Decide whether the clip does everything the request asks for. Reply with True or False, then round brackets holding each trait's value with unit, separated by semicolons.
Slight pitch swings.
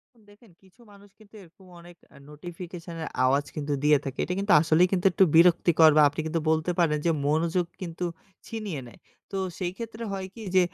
False (3.4 semitones)